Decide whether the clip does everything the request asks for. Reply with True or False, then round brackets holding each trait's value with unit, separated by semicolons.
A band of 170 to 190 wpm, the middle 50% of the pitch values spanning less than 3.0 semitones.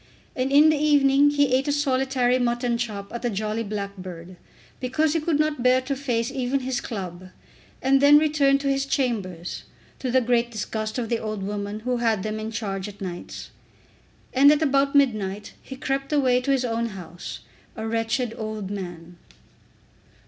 False (180 wpm; 4.5 semitones)